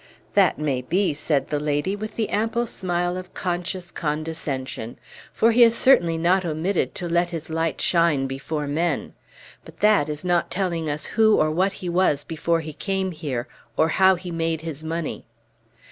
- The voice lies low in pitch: No, medium, 170 Hz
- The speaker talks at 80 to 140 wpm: No, average, 175 wpm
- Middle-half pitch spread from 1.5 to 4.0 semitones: Yes, average, 3.5 semitones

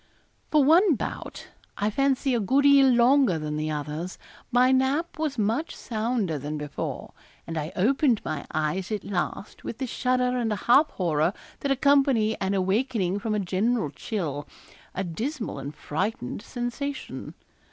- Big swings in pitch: Yes, wide, 7.0 semitones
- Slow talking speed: No, average, 150 wpm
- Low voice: No, high, 220 Hz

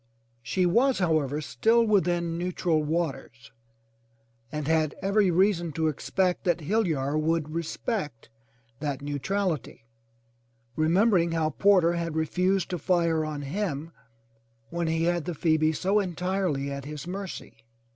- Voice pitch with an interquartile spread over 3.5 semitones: No, average, 3.2 semitones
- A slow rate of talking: Yes, slow, 130 wpm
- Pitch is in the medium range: Yes, medium, 170 Hz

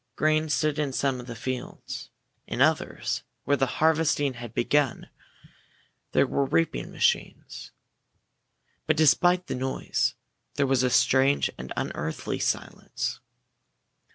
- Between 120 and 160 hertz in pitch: Yes, low, 135 Hz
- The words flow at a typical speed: No, slow, 125 wpm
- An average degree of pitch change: Yes, average, 3.3 semitones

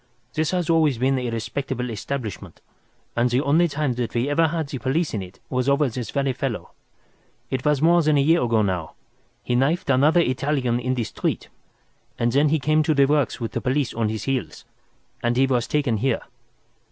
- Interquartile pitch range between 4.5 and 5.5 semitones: No, average, 3.8 semitones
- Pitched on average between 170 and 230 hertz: No, low, 135 Hz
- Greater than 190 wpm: Yes, fast, 205 wpm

